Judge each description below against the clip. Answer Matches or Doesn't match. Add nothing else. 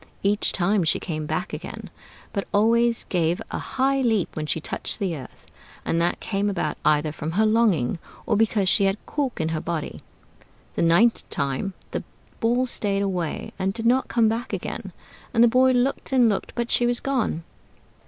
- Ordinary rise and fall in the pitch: Doesn't match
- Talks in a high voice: Matches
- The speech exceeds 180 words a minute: Matches